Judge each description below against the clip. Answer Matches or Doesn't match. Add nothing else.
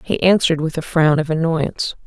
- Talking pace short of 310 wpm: Matches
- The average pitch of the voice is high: Doesn't match